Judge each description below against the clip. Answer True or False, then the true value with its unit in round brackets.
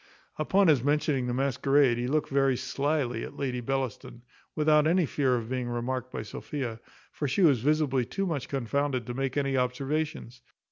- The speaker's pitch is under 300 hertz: True (135 Hz)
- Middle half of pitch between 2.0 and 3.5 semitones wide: True (2.9 semitones)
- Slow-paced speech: False (175 wpm)